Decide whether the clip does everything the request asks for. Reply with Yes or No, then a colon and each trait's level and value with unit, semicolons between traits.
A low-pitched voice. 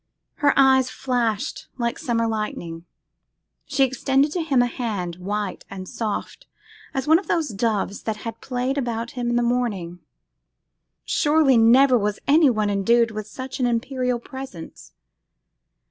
No: high, 240 Hz